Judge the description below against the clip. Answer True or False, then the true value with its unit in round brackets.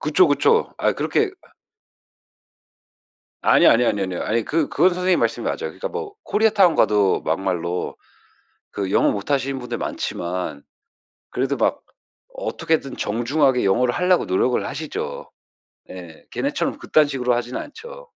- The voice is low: True (130 Hz)